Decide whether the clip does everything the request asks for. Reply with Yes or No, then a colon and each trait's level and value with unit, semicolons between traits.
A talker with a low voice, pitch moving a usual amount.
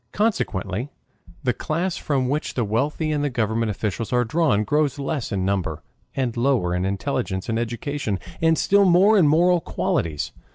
No: low, 125 Hz; wide, 6.5 semitones